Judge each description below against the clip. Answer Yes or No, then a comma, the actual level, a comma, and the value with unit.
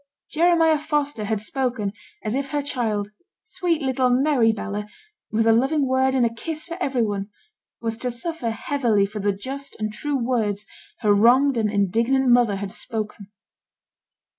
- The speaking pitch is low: No, high, 240 Hz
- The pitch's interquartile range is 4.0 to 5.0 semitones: Yes, average, 4.6 semitones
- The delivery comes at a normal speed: Yes, average, 165 wpm